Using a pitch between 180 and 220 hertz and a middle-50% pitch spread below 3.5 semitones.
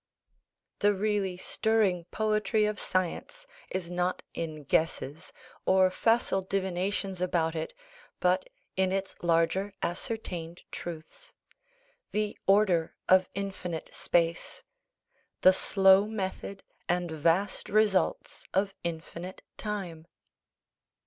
Yes: medium, 185 Hz; average, 2.8 semitones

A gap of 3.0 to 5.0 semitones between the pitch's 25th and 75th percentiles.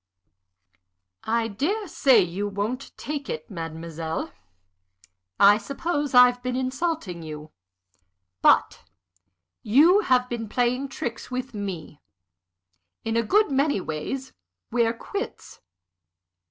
No: wide, 5.5 semitones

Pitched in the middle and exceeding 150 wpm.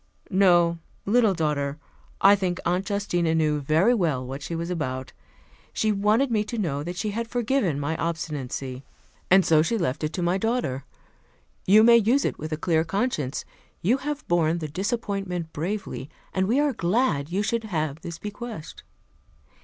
Yes: medium, 175 Hz; average, 170 wpm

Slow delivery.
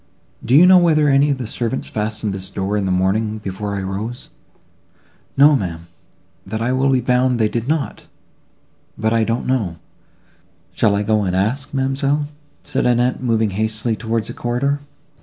No: average, 175 wpm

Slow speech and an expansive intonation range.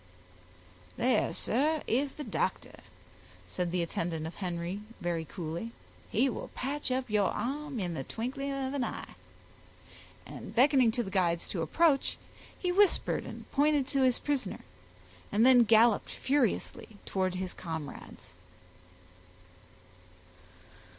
Yes: slow, 130 wpm; wide, 7.2 semitones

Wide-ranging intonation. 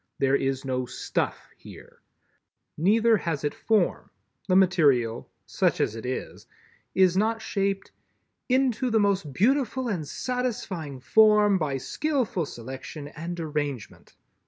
Yes: wide, 7.8 semitones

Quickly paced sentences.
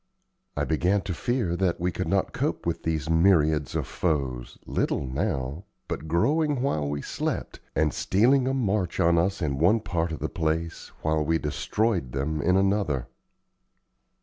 No: average, 165 wpm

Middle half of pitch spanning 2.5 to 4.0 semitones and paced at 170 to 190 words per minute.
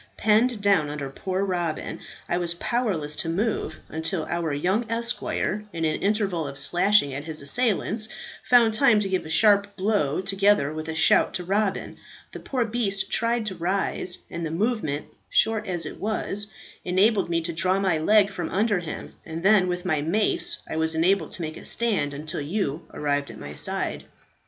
No: average, 4.7 semitones; average, 185 wpm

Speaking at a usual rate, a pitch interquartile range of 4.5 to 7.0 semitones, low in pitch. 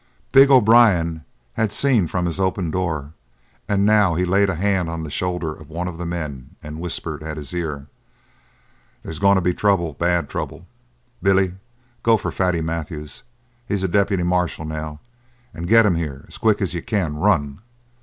No: average, 180 wpm; average, 3.7 semitones; very low, 85 Hz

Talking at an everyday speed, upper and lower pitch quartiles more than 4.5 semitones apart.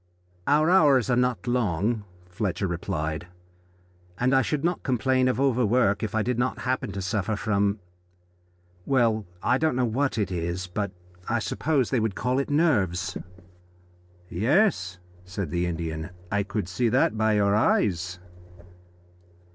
Yes: average, 145 wpm; average, 5.3 semitones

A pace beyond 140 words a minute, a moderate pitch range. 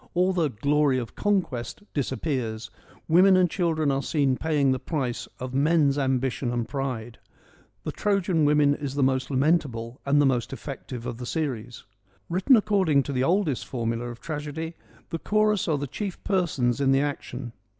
Yes: average, 170 wpm; average, 4.3 semitones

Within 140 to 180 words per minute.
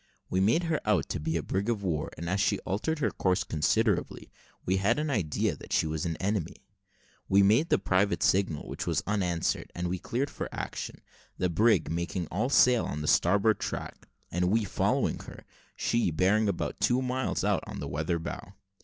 No: average, 195 wpm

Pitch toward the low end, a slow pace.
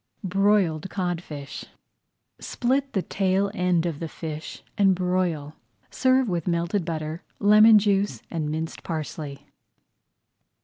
No: medium, 180 Hz; slow, 115 wpm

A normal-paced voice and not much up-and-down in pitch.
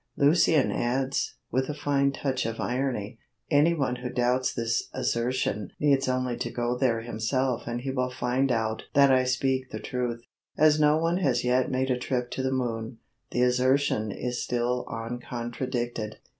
Yes: average, 165 wpm; narrow, 2.0 semitones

